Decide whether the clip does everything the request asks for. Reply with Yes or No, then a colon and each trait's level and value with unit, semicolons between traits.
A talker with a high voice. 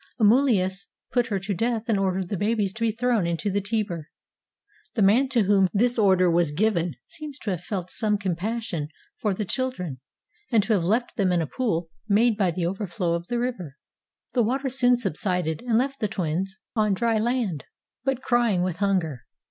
Yes: high, 205 Hz